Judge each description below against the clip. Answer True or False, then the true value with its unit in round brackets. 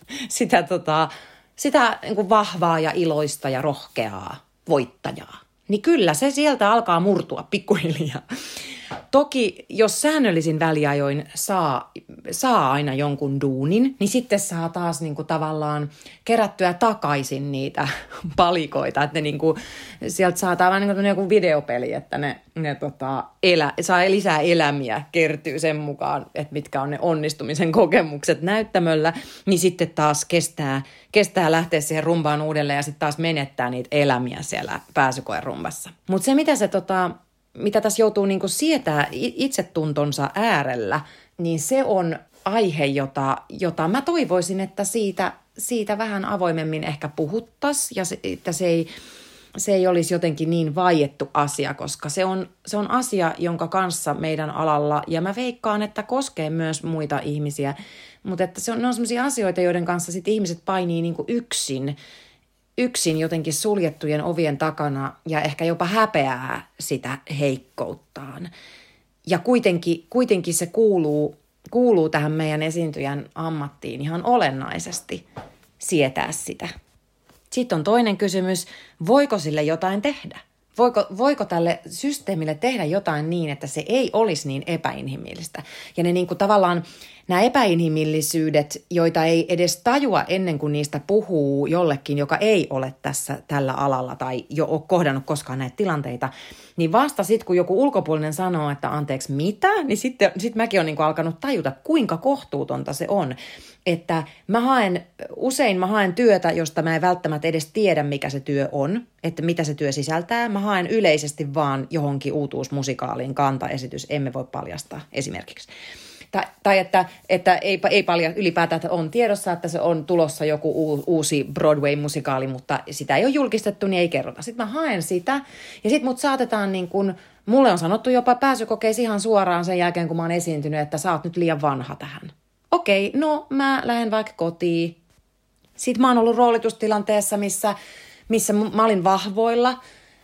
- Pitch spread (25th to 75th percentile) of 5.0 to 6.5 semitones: True (5.5 semitones)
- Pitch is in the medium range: True (170 Hz)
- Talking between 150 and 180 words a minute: True (155 wpm)